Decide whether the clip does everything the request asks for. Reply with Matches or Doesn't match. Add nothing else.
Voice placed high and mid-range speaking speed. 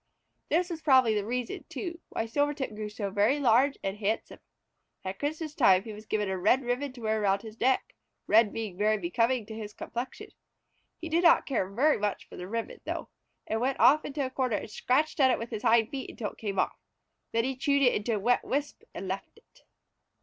Doesn't match